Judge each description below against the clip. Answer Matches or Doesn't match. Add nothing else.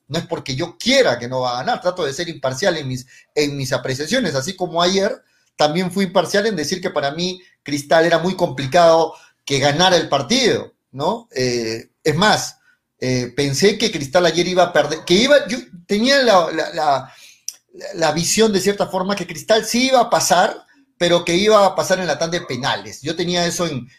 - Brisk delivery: Matches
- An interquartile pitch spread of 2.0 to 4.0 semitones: Doesn't match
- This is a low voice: Doesn't match